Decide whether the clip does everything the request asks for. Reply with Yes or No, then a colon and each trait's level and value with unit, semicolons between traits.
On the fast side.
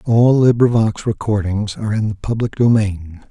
No: average, 145 wpm